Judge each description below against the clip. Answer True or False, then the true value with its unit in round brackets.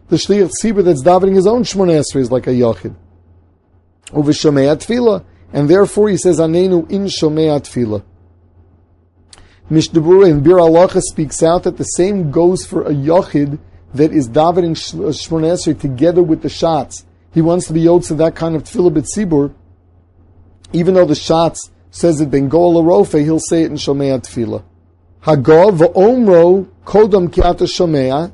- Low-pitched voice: False (160 Hz)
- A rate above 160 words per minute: False (150 wpm)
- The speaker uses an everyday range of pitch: False (6.5 semitones)